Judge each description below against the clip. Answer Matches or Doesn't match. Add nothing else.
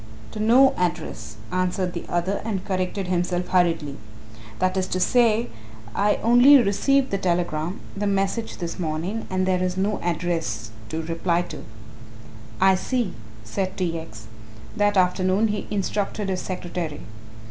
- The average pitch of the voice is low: Doesn't match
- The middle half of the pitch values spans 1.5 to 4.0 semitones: Matches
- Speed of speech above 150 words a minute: Doesn't match